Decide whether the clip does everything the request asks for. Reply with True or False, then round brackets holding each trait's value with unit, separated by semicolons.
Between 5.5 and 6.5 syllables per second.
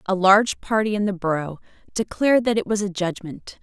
True (5.7 syllables/s)